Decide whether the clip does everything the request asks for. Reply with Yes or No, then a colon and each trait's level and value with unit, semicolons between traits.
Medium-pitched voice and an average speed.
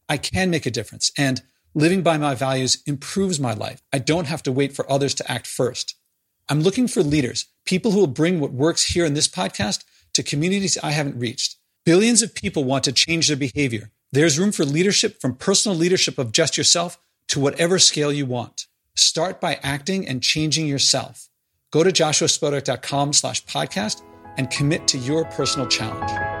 Yes: medium, 150 Hz; average, 185 wpm